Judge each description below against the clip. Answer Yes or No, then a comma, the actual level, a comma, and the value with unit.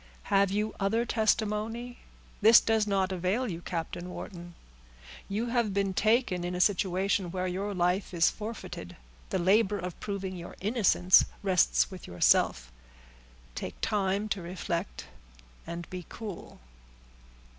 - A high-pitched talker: Yes, high, 195 Hz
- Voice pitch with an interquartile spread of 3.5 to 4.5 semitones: No, average, 2.9 semitones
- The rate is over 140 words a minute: No, slow, 135 wpm